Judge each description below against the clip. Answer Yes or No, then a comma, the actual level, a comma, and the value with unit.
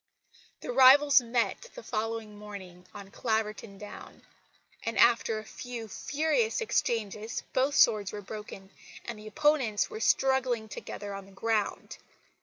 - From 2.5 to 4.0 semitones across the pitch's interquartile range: Yes, average, 3.6 semitones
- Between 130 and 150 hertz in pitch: No, high, 225 Hz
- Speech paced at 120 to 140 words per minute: Yes, slow, 135 wpm